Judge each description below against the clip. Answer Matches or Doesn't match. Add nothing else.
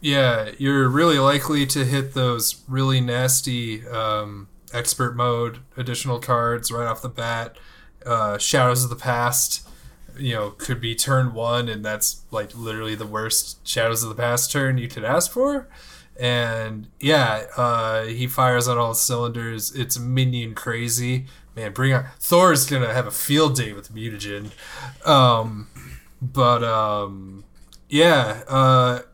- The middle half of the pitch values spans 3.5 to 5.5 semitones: Doesn't match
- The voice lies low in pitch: Matches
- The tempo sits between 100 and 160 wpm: Matches